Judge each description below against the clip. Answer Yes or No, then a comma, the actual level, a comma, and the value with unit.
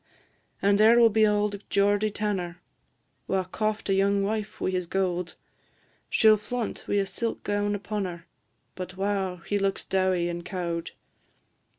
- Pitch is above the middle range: Yes, high, 200 Hz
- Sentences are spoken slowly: No, average, 160 wpm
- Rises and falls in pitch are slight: Yes, narrow, 2.3 semitones